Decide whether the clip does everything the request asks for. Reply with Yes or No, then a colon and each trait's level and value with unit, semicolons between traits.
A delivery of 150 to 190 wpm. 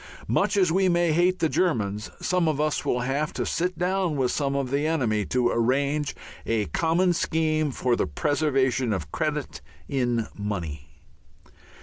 Yes: average, 160 wpm